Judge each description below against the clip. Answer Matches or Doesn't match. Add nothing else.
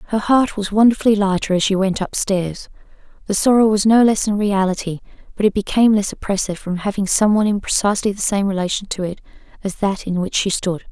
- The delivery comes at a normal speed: Doesn't match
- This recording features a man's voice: Doesn't match